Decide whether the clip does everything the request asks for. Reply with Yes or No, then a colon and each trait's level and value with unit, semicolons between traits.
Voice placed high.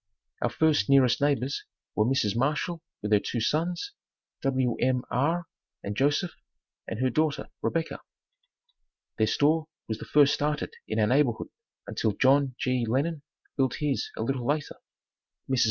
No: low, 135 Hz